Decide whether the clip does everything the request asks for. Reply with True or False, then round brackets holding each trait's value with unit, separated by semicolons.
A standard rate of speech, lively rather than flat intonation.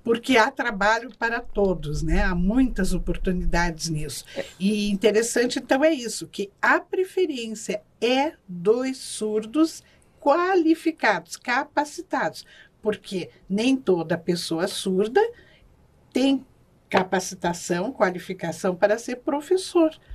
False (100 wpm; 6.7 semitones)